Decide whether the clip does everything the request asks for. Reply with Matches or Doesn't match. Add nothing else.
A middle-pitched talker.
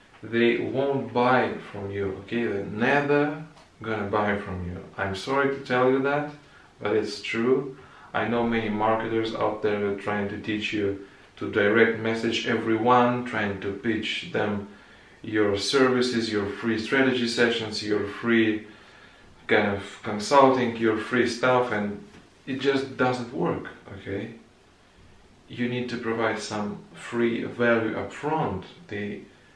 Doesn't match